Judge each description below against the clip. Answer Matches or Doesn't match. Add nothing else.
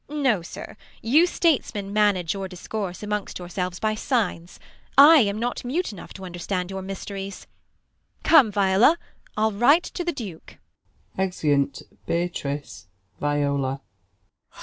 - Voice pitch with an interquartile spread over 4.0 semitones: Matches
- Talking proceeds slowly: Matches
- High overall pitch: Matches